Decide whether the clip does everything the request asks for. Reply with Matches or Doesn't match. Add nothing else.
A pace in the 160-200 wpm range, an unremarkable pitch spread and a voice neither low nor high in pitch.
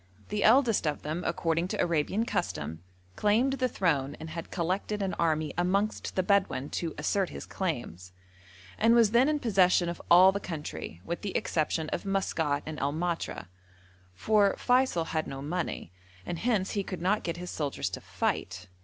Matches